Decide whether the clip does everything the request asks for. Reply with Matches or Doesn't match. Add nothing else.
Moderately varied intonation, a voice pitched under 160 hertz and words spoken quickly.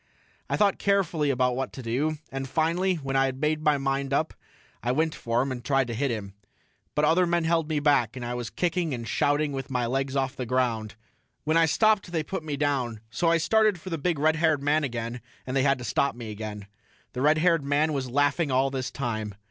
Matches